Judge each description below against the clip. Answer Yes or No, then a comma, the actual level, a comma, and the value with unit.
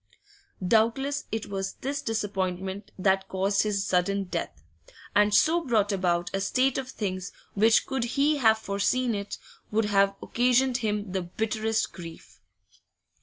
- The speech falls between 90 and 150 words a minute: Yes, average, 140 wpm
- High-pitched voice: Yes, high, 210 Hz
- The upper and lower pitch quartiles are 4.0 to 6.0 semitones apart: No, average, 3.5 semitones